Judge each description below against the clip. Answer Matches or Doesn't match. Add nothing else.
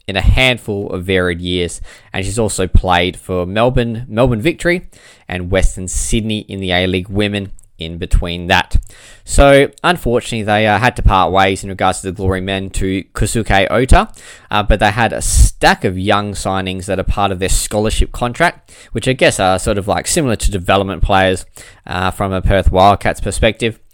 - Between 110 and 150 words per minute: Doesn't match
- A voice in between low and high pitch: Doesn't match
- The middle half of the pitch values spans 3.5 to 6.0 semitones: Doesn't match